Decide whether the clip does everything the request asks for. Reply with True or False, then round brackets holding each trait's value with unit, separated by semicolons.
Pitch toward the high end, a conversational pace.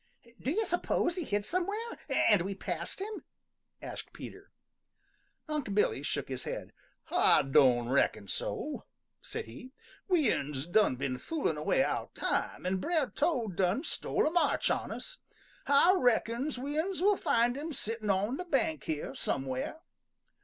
True (240 Hz; 155 wpm)